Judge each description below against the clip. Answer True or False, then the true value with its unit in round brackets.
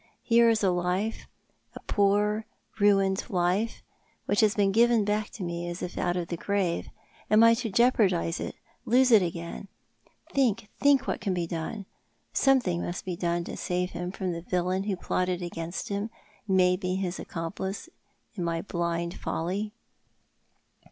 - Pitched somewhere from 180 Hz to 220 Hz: True (190 Hz)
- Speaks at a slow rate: False (165 wpm)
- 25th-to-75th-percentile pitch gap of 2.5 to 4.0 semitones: True (3.3 semitones)